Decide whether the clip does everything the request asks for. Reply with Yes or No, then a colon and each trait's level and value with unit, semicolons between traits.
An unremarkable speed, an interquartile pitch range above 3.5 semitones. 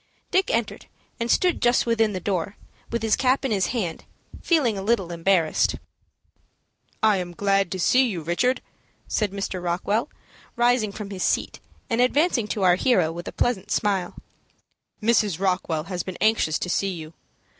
Yes: average, 165 wpm; average, 4.6 semitones